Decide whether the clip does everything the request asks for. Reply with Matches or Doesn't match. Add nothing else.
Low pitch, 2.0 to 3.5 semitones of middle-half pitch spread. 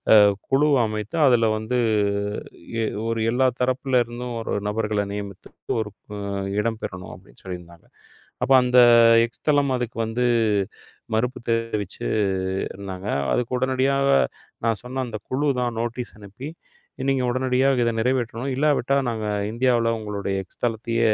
Matches